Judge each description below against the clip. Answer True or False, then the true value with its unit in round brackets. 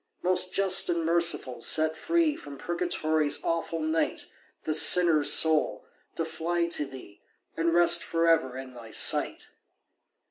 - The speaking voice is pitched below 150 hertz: False (165 Hz)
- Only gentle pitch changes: True (2.3 semitones)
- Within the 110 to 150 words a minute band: True (140 wpm)